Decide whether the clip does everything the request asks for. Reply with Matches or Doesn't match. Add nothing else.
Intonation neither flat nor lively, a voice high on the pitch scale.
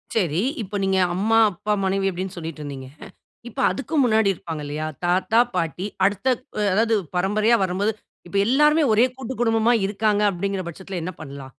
Matches